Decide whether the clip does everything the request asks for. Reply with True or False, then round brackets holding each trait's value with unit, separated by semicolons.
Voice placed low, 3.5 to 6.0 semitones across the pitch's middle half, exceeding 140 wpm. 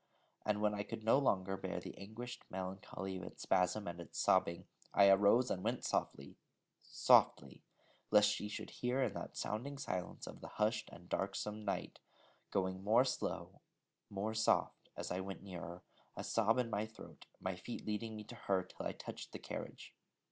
False (100 Hz; 2.8 semitones; 180 wpm)